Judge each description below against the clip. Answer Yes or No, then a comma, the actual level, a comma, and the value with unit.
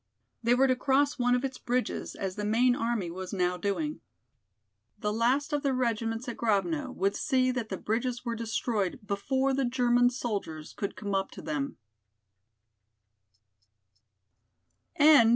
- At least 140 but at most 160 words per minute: Yes, average, 150 wpm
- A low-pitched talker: No, high, 235 Hz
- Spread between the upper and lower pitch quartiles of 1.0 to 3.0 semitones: No, average, 4.1 semitones